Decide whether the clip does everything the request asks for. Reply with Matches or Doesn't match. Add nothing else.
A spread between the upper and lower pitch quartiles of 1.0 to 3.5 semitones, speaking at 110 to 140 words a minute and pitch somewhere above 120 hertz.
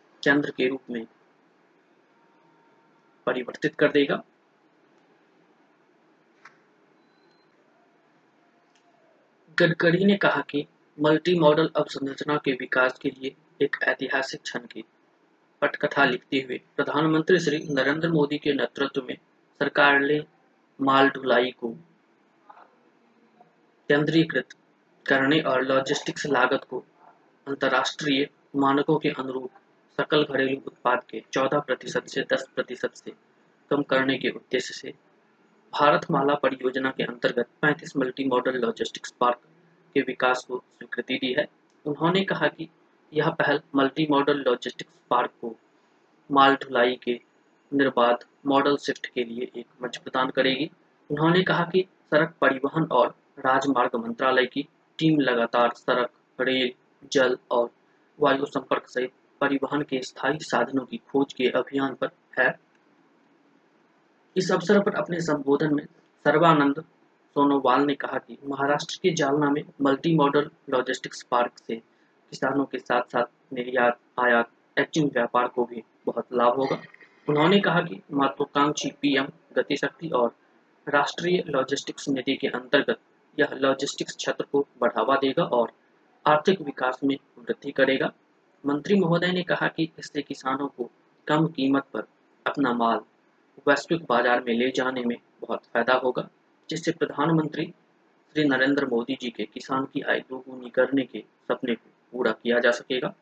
Matches